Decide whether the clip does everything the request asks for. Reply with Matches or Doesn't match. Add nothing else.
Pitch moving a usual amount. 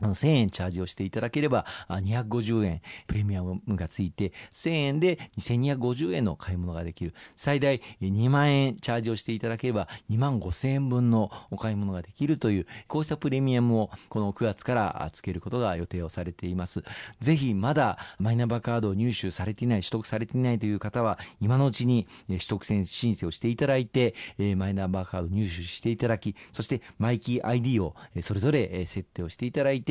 Matches